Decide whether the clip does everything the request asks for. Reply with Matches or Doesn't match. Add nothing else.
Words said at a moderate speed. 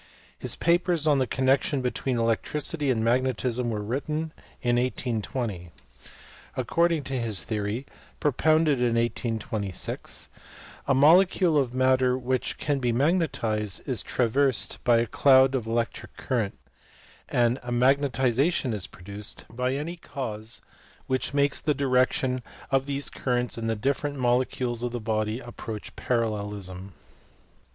Doesn't match